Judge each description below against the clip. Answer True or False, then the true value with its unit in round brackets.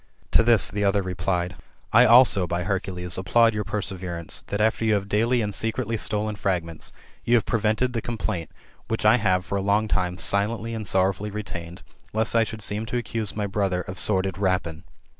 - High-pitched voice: False (100 Hz)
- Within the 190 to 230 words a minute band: True (195 wpm)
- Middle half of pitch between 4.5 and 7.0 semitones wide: False (3.2 semitones)